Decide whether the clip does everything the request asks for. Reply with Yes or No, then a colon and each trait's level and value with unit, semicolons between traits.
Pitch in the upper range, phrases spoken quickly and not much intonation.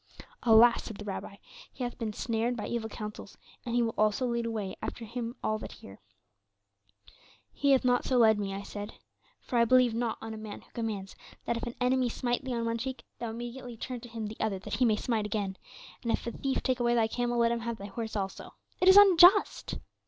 Yes: high, 230 Hz; fast, 230 wpm; narrow, 2.1 semitones